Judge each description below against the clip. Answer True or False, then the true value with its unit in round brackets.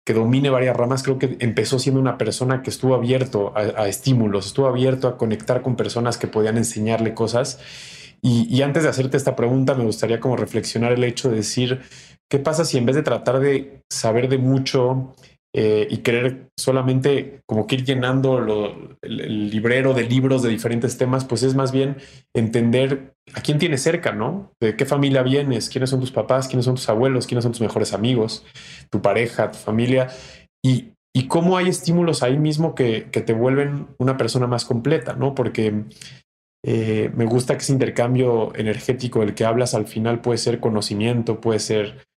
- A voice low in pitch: True (125 Hz)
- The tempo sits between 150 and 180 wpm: False (190 wpm)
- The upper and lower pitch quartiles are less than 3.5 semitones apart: True (2.7 semitones)